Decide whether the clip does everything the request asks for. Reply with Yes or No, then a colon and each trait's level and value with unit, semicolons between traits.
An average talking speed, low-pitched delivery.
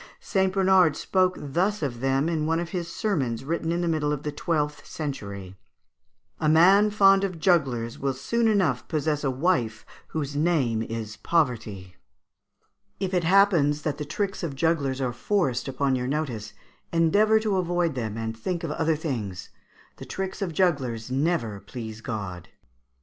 No: average, 170 wpm; medium, 150 Hz